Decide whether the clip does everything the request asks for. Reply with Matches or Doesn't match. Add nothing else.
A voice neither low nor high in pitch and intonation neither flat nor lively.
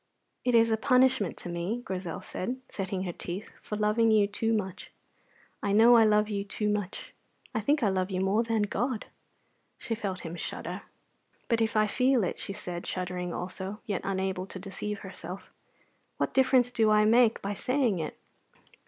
Doesn't match